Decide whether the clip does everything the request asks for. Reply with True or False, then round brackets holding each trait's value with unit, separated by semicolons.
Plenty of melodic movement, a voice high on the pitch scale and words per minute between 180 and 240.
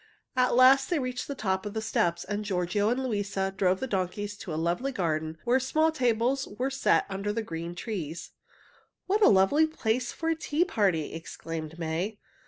True (6.4 semitones; 210 Hz; 190 wpm)